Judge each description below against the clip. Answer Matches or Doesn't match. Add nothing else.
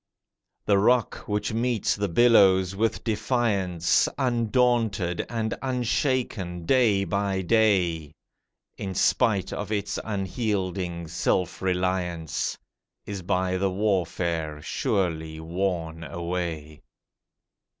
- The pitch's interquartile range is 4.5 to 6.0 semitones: Doesn't match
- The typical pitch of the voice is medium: Doesn't match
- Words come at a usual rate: Doesn't match